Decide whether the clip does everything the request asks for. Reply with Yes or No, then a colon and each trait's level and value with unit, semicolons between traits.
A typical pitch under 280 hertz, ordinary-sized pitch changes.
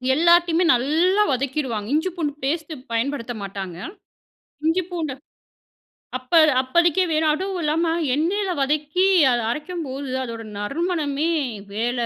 No: very high, 300 Hz; average, 5.0 semitones